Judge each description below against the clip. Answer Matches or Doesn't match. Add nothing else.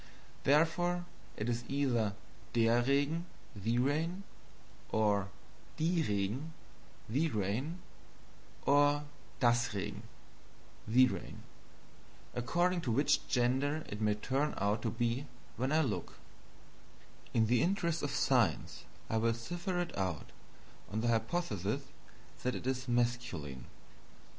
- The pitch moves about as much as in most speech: Matches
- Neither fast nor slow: Doesn't match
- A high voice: Doesn't match